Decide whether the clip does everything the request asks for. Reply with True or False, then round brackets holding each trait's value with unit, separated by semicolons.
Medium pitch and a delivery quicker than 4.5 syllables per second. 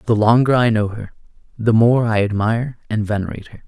False (110 Hz; 6.0 syllables/s)